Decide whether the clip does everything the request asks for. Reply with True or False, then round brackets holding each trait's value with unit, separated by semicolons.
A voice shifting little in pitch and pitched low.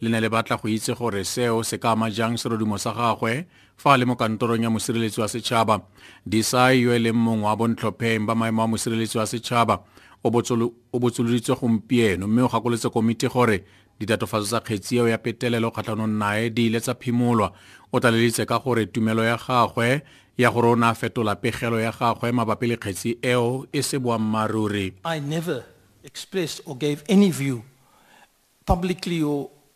True (1.8 semitones; 115 Hz)